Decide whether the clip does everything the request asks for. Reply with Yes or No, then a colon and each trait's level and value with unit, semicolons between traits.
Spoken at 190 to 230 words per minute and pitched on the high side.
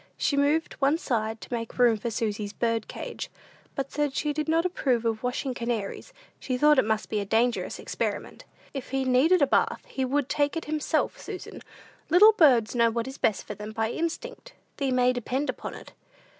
Yes: average, 200 wpm; very high, 255 Hz